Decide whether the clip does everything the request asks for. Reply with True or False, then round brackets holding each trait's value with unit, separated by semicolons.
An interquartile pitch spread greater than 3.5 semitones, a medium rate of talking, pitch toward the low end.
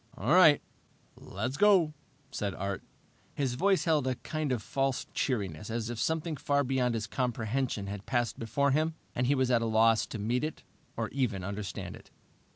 True (4.5 semitones; 180 wpm; 125 Hz)